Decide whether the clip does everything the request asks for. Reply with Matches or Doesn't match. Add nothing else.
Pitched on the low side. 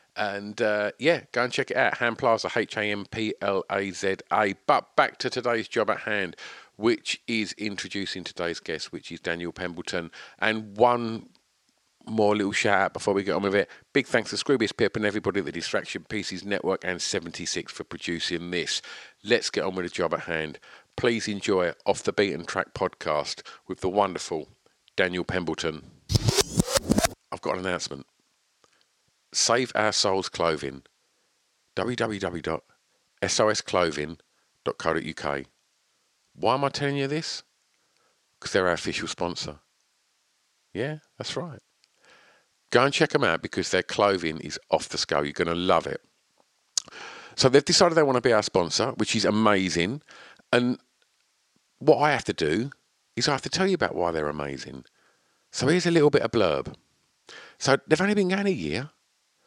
Matches